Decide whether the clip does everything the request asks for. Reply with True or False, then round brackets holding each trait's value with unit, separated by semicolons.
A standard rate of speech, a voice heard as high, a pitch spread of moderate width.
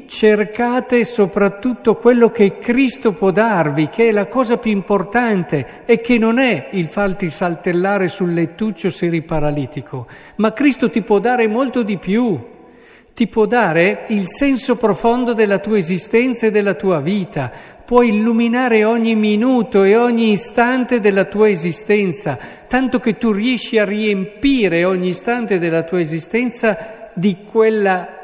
True (145 wpm; 215 Hz; 4.0 semitones)